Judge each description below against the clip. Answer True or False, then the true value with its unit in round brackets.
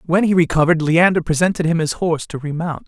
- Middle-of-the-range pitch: True (165 Hz)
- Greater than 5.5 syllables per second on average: True (6.4 syllables/s)